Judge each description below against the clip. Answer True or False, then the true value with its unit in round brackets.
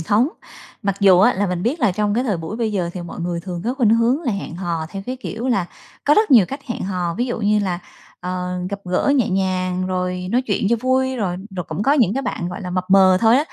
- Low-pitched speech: False (200 Hz)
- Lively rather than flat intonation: False (4.8 semitones)